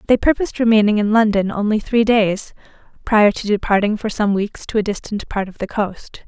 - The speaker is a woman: Yes, female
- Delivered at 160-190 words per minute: No, average, 200 wpm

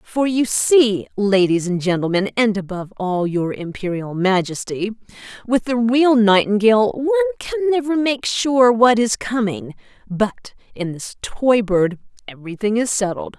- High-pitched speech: Yes, high, 220 Hz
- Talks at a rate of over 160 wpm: No, average, 145 wpm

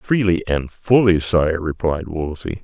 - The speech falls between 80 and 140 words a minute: Yes, slow, 135 wpm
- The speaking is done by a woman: No, male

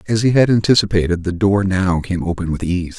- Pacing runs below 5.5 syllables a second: No, 5.7 syllables/s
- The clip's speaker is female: No, male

